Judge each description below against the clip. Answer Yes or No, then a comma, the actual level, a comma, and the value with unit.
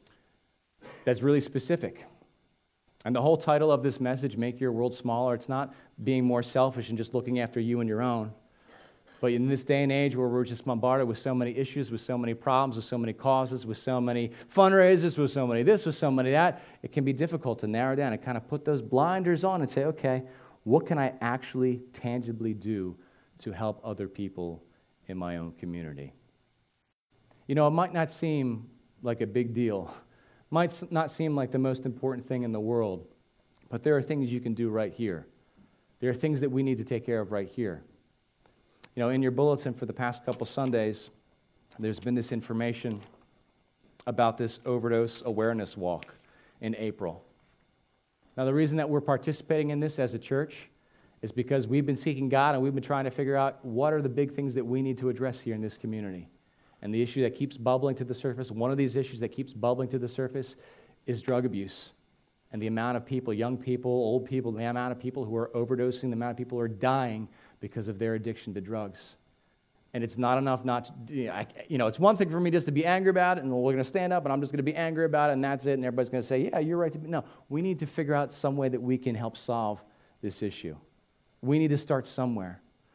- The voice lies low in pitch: Yes, low, 125 Hz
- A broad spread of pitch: No, average, 3.1 semitones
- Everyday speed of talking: No, fast, 225 wpm